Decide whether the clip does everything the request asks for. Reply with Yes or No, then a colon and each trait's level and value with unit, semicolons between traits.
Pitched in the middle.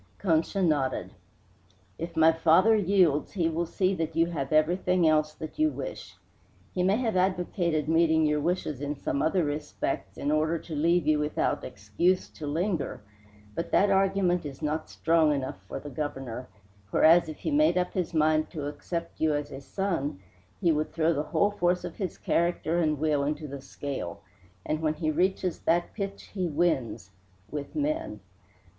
Yes: medium, 160 Hz